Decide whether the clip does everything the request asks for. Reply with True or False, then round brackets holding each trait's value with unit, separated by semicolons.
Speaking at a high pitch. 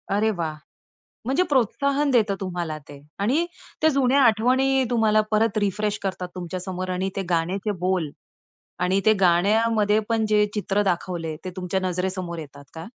True (200 Hz)